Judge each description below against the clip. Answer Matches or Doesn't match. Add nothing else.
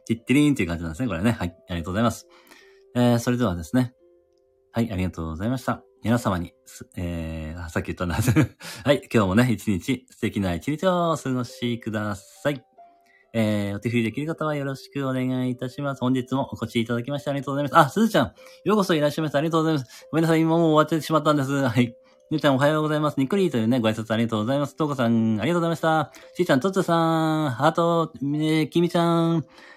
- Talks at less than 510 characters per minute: Doesn't match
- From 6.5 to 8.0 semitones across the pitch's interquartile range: Doesn't match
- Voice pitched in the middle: Doesn't match